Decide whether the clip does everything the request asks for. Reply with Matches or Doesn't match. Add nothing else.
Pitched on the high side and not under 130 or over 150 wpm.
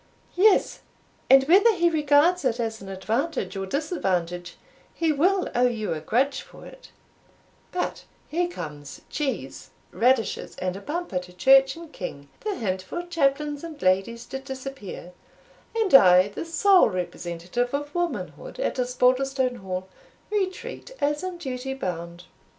Matches